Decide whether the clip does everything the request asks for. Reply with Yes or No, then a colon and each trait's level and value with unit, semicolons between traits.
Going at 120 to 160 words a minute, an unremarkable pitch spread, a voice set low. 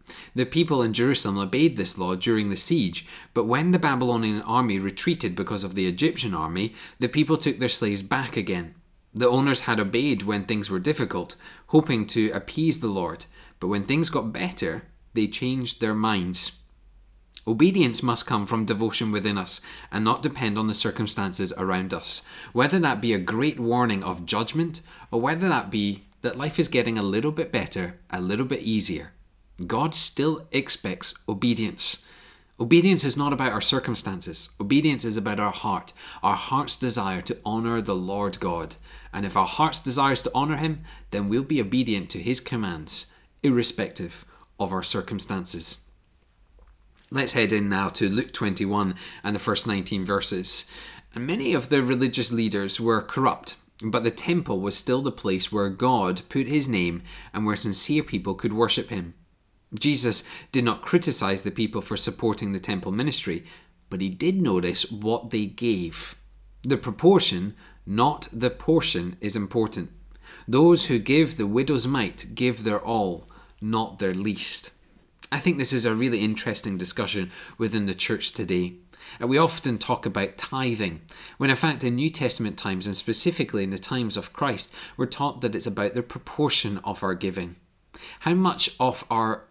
No: average, 170 wpm; average, 4.8 semitones; low, 115 Hz